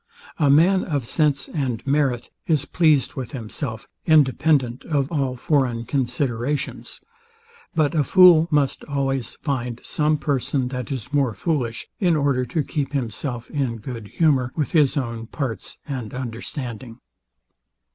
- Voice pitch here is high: No, low, 135 Hz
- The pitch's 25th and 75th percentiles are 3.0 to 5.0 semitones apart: Yes, average, 3.4 semitones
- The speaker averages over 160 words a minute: No, slow, 135 wpm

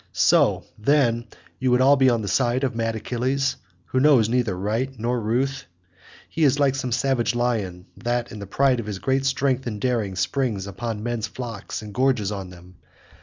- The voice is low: Yes, low, 120 Hz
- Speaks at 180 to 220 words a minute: Yes, average, 190 wpm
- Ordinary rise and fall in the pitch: Yes, average, 3.6 semitones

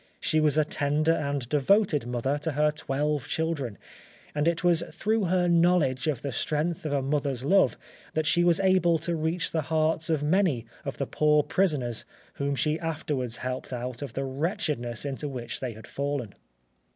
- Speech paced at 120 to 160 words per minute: No, average, 180 wpm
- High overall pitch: No, medium, 150 Hz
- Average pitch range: Yes, average, 3.4 semitones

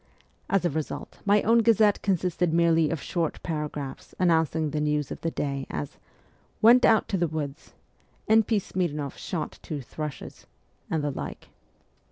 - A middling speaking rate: Yes, average, 165 wpm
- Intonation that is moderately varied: Yes, average, 4.1 semitones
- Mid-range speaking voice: Yes, medium, 165 Hz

